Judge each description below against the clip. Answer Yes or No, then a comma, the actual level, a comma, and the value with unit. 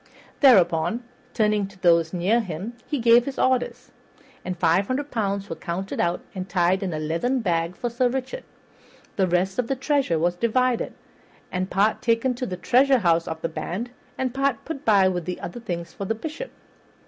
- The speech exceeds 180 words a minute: Yes, average, 190 wpm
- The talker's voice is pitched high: Yes, high, 200 Hz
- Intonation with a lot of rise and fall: Yes, wide, 5.9 semitones